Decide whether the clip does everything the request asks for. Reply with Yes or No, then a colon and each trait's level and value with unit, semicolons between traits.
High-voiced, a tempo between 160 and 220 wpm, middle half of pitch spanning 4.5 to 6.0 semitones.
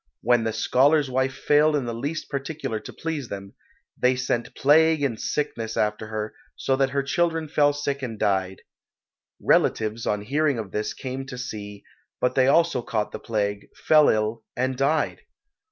No: low, 130 Hz; average, 170 wpm; average, 4.9 semitones